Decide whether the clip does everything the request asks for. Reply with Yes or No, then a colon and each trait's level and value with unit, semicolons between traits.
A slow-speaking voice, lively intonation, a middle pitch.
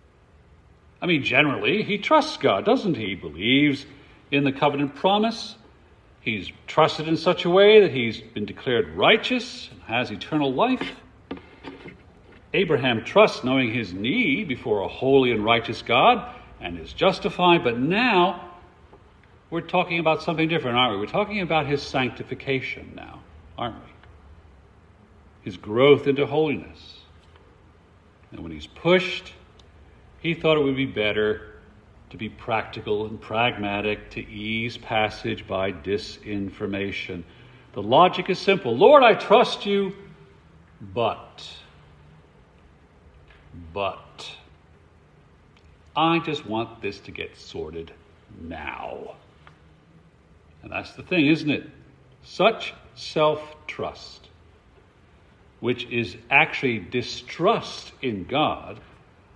No: slow, 120 wpm; wide, 8.1 semitones; low, 115 Hz